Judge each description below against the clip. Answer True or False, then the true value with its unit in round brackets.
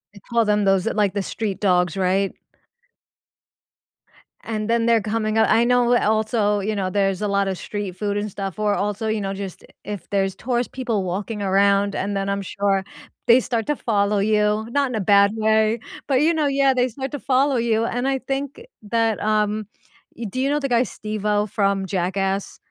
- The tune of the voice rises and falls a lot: False (2.9 semitones)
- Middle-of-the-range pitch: False (210 Hz)